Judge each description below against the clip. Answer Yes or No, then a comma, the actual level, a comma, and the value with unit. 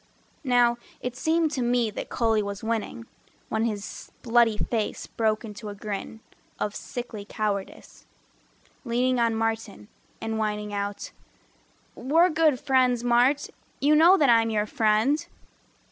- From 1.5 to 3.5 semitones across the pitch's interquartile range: Yes, average, 2.9 semitones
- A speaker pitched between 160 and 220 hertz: No, high, 230 Hz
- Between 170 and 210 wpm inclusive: No, slow, 135 wpm